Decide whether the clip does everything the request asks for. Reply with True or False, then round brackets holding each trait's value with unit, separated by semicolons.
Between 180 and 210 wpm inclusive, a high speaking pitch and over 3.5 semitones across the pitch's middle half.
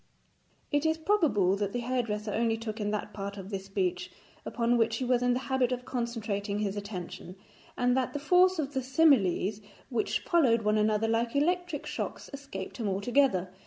True (185 wpm; 230 Hz; 4.4 semitones)